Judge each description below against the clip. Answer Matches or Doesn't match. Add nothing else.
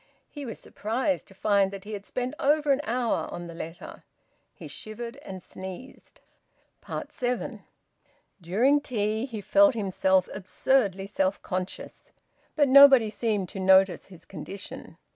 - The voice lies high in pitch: Matches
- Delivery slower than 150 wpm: Matches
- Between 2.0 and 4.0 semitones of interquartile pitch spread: Doesn't match